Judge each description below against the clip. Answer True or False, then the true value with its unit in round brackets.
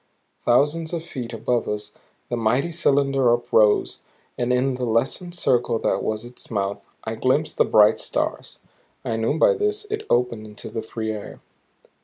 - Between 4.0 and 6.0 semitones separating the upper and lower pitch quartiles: True (4.3 semitones)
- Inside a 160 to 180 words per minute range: True (165 wpm)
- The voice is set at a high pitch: False (120 Hz)